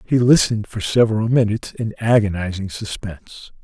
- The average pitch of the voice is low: Yes, low, 105 Hz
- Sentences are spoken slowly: Yes, slow, 130 wpm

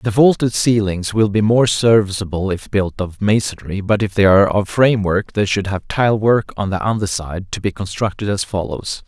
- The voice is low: Yes, low, 100 Hz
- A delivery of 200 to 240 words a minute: Yes, fast, 205 wpm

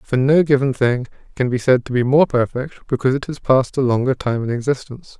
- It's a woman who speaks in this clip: No, male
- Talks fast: Yes, fast, 230 wpm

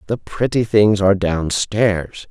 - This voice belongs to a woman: No, male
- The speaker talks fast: No, slow, 130 wpm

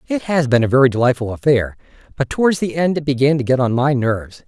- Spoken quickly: Yes, fast, 240 wpm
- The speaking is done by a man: Yes, male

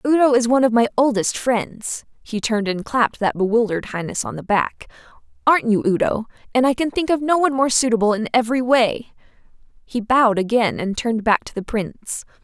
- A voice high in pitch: Yes, high, 230 Hz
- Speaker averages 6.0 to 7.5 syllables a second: Yes, 6.1 syllables/s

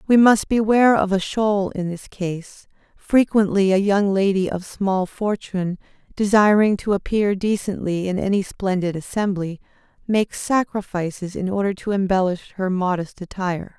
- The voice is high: Yes, high, 195 Hz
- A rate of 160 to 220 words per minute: No, average, 145 wpm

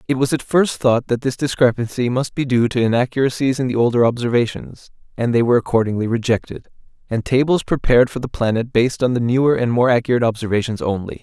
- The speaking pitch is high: No, low, 120 Hz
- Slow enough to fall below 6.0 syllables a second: No, 6.5 syllables/s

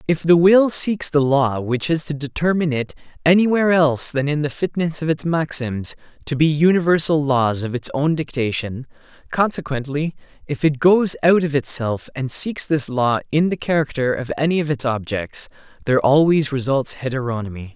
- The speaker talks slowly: No, average, 170 wpm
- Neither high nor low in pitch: Yes, medium, 145 Hz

